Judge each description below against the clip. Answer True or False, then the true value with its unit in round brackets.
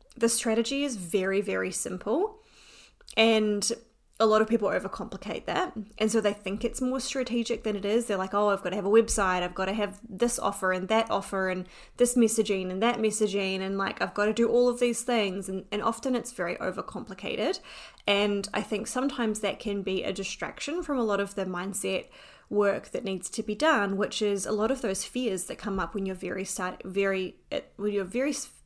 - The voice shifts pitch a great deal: False (3.0 semitones)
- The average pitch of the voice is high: True (210 Hz)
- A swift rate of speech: True (215 wpm)